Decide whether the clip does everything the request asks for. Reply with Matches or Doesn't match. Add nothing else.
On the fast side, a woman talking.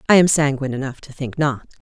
Matches